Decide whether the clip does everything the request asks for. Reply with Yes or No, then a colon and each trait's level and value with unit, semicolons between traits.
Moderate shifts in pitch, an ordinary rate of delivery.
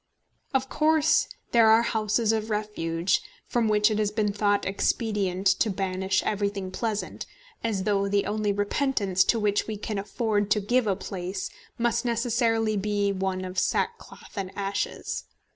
No: narrow, 2.3 semitones; average, 155 wpm